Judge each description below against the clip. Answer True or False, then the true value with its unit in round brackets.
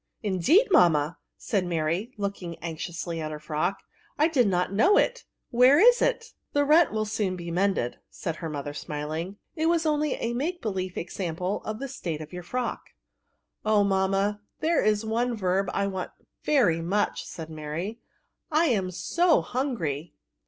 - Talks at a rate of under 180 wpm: False (185 wpm)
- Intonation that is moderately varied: False (7.0 semitones)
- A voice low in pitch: False (195 Hz)